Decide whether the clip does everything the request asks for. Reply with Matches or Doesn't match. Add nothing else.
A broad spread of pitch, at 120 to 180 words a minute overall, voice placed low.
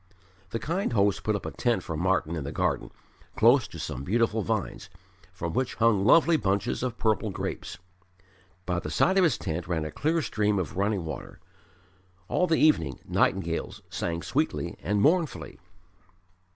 Matches